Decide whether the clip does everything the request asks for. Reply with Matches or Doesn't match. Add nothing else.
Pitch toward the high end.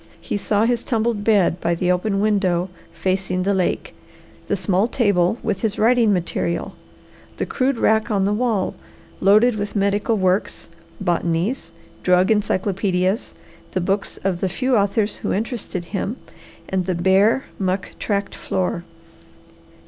Matches